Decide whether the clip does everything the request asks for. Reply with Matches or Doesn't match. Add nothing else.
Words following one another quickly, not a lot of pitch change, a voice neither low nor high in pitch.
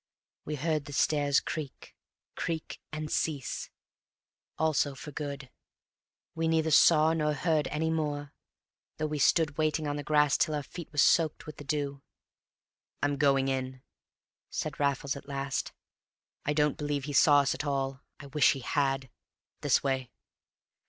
Doesn't match